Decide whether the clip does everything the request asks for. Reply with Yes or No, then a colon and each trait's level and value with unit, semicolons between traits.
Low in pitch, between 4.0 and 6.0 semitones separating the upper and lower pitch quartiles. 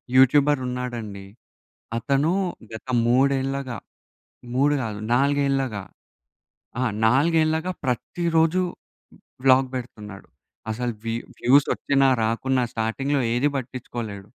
No: low, 130 Hz; average, 3.2 semitones